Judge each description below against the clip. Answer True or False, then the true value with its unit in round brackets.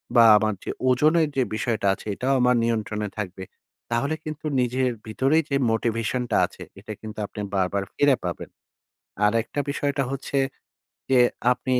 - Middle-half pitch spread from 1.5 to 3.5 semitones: False (4.1 semitones)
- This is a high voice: False (120 Hz)